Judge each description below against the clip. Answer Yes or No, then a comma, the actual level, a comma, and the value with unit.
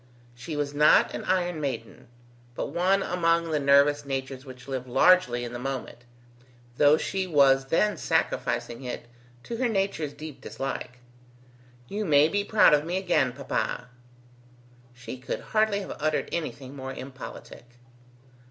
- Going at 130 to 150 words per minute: Yes, average, 145 wpm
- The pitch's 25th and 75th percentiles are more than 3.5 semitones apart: Yes, average, 5.1 semitones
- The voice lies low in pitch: No, medium, 145 Hz